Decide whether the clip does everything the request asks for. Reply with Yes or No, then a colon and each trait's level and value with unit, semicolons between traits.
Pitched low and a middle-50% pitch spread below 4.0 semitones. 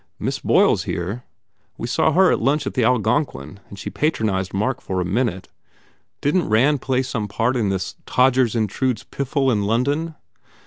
No: low, 120 Hz; average, 4.7 semitones